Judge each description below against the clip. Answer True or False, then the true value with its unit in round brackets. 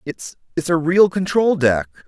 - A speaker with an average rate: True (145 wpm)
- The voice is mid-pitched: True (160 Hz)